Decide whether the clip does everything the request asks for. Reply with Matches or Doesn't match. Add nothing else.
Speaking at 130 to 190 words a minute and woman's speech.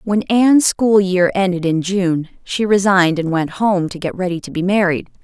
Doesn't match